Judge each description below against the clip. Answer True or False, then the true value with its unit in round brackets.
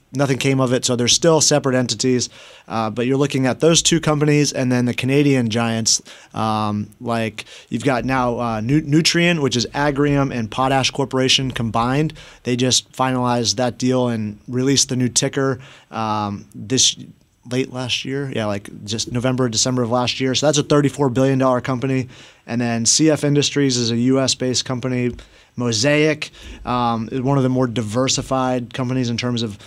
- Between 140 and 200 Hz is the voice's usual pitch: False (130 Hz)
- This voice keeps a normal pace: True (175 wpm)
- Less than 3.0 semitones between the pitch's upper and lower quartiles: True (2.5 semitones)